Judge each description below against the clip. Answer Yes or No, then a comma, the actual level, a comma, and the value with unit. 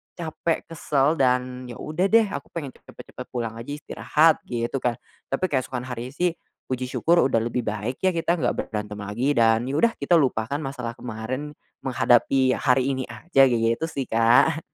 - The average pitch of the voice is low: Yes, low, 130 Hz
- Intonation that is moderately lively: Yes, average, 4.2 semitones